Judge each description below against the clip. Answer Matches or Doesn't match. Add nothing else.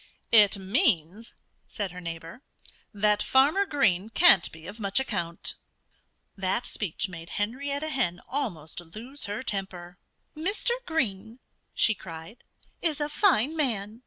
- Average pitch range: Doesn't match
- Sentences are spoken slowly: Matches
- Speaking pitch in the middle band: Doesn't match